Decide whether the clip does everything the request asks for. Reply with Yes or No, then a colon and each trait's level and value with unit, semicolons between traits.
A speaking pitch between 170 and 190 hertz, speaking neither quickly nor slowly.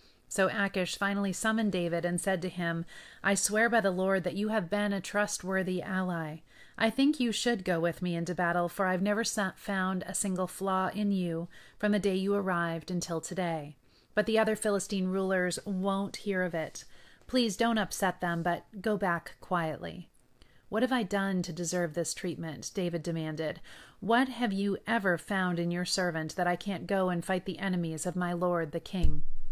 Yes: medium, 185 Hz; average, 190 wpm